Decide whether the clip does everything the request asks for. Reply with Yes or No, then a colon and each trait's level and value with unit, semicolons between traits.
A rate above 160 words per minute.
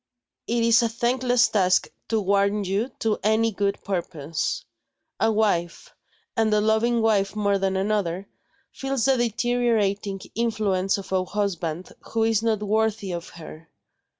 No: average, 145 wpm